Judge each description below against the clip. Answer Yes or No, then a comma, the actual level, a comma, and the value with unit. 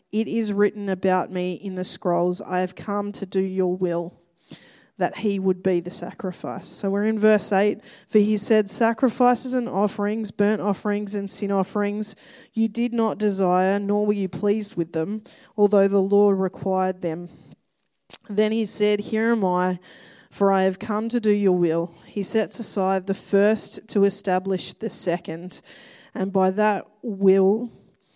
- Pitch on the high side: Yes, high, 200 Hz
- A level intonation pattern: Yes, narrow, 2.3 semitones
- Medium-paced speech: Yes, average, 170 wpm